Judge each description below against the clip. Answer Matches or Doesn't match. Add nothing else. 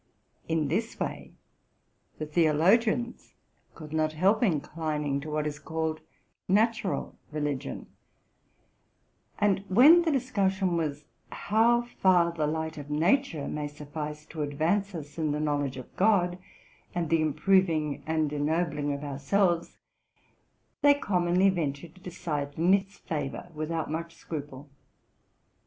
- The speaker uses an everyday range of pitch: Matches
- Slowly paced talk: Matches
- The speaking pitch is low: Doesn't match